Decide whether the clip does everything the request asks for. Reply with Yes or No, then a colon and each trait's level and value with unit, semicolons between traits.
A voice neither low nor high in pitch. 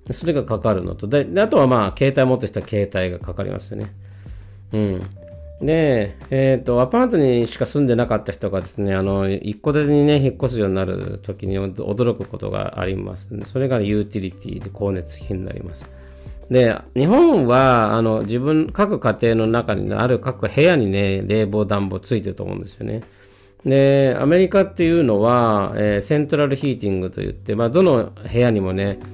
No: low, 110 Hz